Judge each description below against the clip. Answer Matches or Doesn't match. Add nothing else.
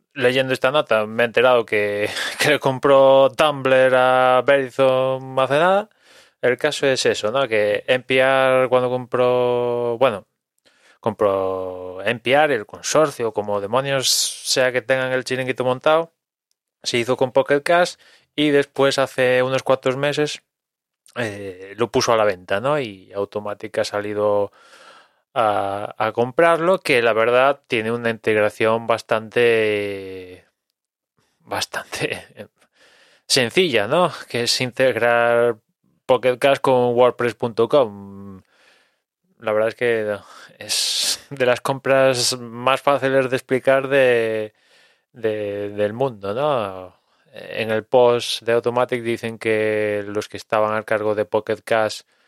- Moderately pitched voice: Doesn't match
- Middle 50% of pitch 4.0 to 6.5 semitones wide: Doesn't match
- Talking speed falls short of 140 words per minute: Matches